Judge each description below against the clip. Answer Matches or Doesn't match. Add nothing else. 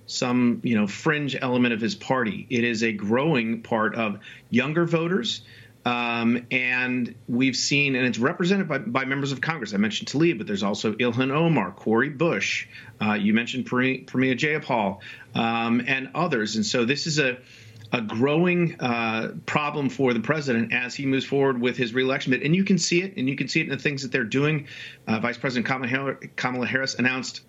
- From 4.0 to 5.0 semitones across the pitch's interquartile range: Doesn't match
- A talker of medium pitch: Doesn't match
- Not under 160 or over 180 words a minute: Doesn't match